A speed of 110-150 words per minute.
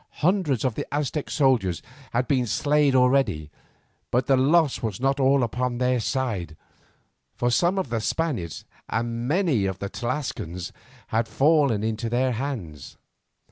Yes: average, 145 wpm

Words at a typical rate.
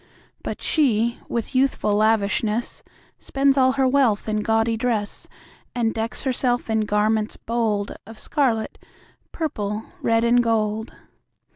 No: slow, 125 wpm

